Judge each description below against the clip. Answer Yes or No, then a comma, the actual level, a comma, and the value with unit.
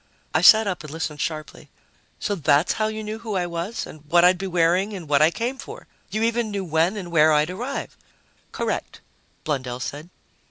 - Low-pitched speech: No, medium, 175 Hz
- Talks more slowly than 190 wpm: No, average, 200 wpm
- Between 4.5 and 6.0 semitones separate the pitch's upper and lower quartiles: Yes, wide, 5.5 semitones